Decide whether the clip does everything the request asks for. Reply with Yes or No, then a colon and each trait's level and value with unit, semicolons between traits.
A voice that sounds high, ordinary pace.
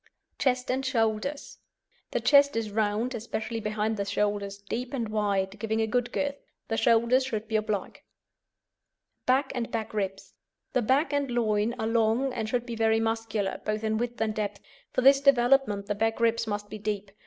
Yes: high, 225 Hz; average, 180 wpm